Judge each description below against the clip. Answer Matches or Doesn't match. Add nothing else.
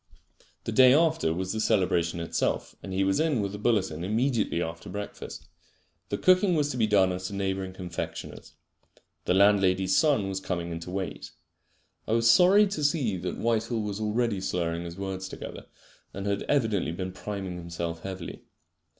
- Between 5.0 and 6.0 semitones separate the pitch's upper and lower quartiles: Doesn't match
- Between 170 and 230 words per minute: Matches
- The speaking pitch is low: Matches